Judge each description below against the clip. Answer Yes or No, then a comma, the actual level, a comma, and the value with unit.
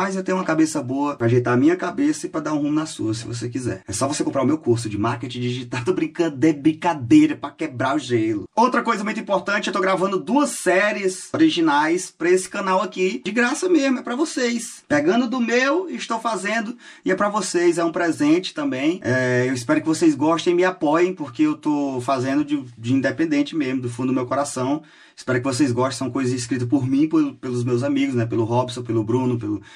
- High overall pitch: No, medium, 175 Hz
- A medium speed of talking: No, fast, 230 wpm